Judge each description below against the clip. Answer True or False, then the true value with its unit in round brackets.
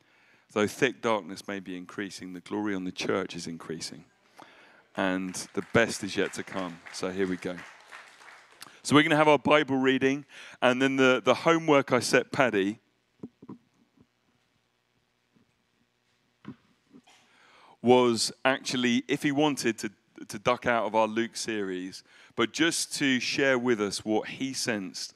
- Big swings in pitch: True (5.7 semitones)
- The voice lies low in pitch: True (115 Hz)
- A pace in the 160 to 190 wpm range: False (150 wpm)